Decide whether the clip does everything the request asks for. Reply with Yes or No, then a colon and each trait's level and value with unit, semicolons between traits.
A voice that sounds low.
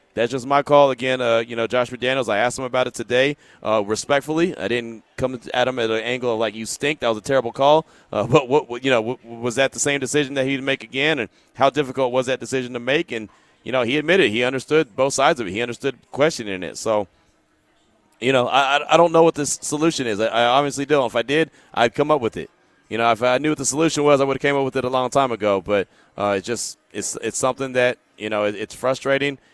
Yes: low, 130 Hz